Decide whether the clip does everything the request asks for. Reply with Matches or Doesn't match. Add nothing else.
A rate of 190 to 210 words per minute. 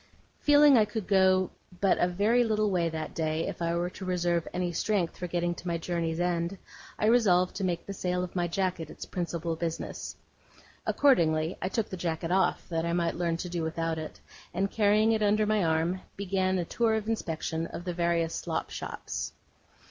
Matches